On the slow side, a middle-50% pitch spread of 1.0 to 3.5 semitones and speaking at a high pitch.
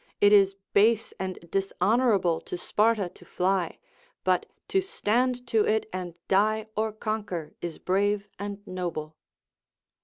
Yes: slow, 130 wpm; average, 2.9 semitones; high, 205 Hz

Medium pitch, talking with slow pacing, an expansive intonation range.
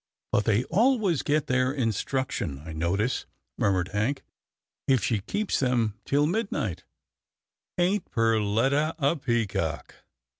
No: low, 125 Hz; slow, 125 wpm; wide, 6.3 semitones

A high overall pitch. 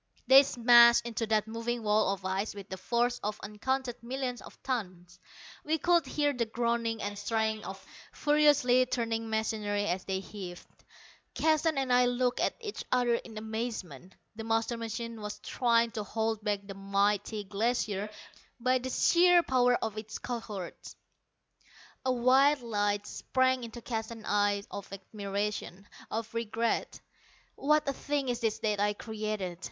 Yes: high, 225 Hz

